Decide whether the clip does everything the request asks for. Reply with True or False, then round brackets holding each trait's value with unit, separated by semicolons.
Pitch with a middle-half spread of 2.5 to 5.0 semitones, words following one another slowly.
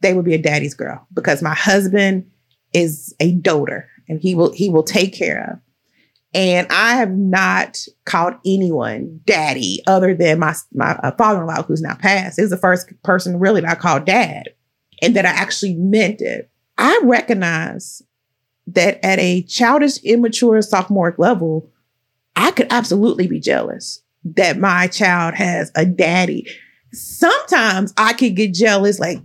False (3.9 semitones; 160 wpm)